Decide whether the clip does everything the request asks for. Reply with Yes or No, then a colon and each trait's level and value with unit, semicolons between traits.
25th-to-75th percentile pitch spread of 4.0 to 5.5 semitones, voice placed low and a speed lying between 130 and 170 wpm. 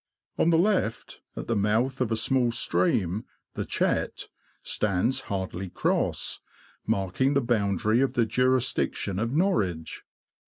Yes: average, 4.8 semitones; low, 115 Hz; slow, 135 wpm